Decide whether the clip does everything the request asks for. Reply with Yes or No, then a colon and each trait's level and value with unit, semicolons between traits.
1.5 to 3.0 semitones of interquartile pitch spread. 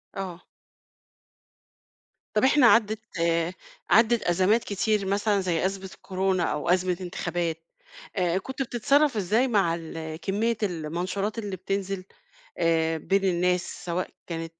No: average, 3.6 semitones